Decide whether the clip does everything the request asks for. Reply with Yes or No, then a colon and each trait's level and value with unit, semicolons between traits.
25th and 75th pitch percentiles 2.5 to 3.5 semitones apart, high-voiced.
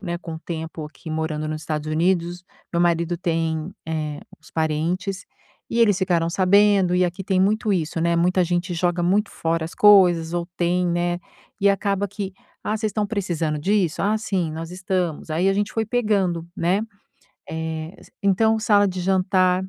No: average, 3.2 semitones; medium, 180 Hz